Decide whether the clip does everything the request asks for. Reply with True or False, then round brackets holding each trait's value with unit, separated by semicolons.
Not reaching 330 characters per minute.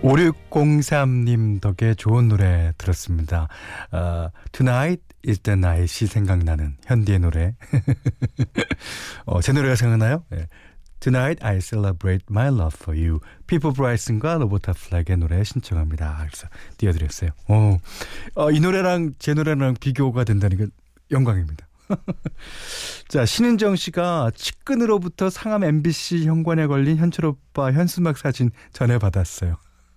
False (335 characters per minute)